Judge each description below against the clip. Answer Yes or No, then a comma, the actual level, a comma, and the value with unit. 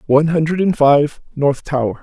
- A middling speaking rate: Yes, average, 180 wpm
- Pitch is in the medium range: Yes, medium, 145 Hz